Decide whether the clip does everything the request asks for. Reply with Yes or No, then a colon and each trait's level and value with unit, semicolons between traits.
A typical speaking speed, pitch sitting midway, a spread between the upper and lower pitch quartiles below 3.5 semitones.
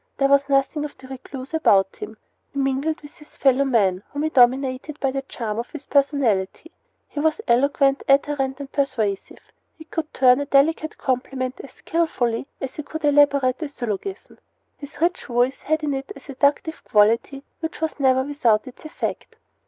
No: average, 175 wpm; very high, 275 Hz; narrow, 2.4 semitones